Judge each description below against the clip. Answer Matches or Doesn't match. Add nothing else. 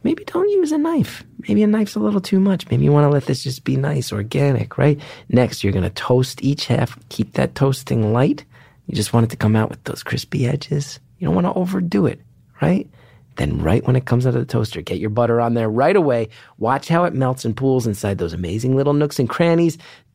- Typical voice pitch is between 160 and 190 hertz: Doesn't match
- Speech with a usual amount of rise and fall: Matches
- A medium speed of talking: Doesn't match